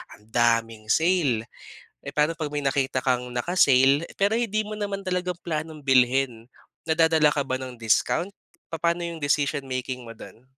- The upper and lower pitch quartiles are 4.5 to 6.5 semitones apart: Yes, average, 5.0 semitones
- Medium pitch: Yes, medium, 145 Hz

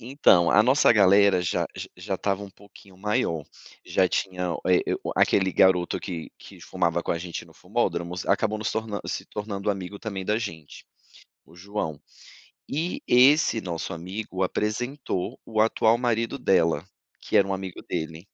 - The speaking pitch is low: Yes, very low, 95 Hz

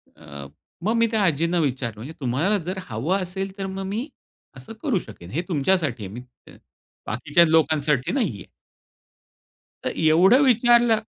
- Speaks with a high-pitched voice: No, medium, 165 Hz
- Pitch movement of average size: No, wide, 7.2 semitones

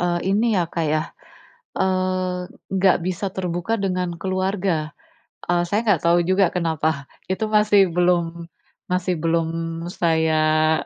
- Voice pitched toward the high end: No, medium, 180 Hz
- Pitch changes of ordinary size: No, narrow, 2.2 semitones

